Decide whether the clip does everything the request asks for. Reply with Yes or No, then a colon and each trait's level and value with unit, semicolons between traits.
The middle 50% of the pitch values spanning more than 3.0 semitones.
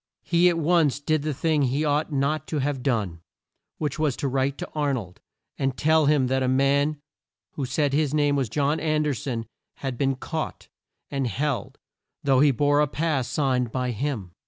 No: narrow, 2.5 semitones